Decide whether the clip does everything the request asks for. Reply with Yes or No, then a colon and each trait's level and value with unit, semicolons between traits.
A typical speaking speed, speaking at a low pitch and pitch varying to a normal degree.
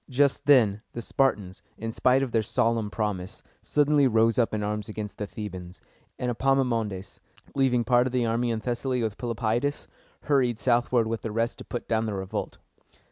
Yes: average, 180 wpm; low, 115 Hz; average, 3.0 semitones